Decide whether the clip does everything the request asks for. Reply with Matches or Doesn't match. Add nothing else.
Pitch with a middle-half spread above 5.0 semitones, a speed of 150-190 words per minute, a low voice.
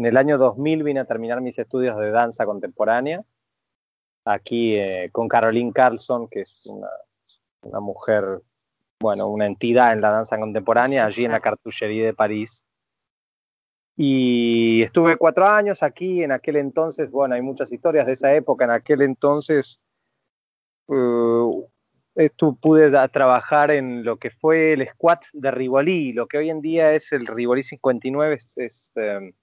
Doesn't match